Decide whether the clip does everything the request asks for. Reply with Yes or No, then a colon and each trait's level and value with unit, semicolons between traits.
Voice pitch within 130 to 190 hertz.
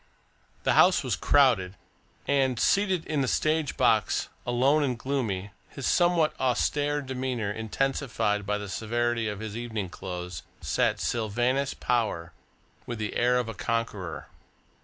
No: low, 120 Hz